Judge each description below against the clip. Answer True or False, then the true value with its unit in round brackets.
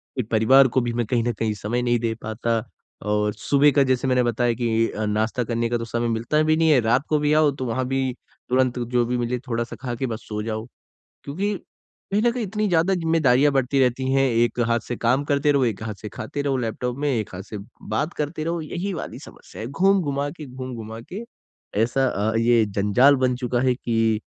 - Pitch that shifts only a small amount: False (3.7 semitones)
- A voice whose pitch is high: False (125 Hz)